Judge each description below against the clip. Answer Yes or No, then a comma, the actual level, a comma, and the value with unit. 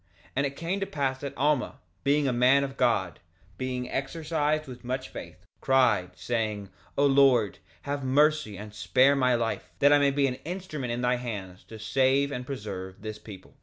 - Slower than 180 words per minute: No, average, 190 wpm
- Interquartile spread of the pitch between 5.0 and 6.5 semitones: No, average, 4.0 semitones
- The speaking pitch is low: Yes, low, 130 Hz